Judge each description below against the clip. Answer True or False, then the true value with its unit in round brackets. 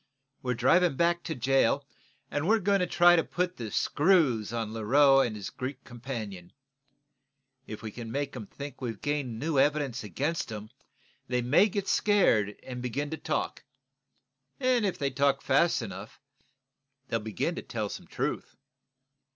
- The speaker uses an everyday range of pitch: False (6.1 semitones)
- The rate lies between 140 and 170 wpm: True (160 wpm)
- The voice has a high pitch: False (135 Hz)